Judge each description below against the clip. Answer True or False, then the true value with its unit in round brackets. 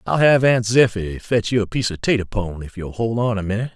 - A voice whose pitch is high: False (110 Hz)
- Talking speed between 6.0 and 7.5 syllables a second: True (6.1 syllables/s)